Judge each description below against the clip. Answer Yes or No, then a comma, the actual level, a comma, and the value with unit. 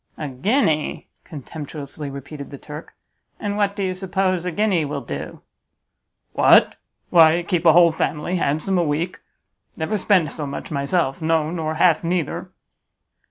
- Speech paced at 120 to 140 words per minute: No, average, 150 wpm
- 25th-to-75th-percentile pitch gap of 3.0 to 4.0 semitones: Yes, average, 3.5 semitones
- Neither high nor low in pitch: Yes, medium, 160 Hz